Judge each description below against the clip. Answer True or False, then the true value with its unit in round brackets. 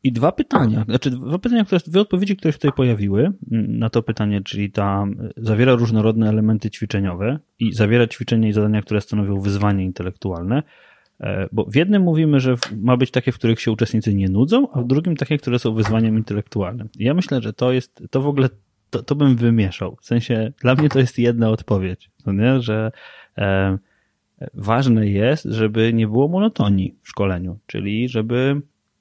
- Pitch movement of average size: True (4.1 semitones)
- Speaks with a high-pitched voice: False (115 Hz)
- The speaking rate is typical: False (180 wpm)